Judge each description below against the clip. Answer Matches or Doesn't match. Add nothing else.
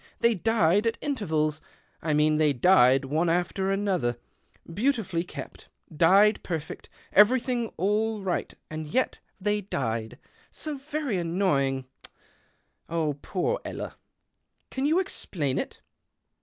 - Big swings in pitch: Matches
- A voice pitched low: Doesn't match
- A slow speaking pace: Matches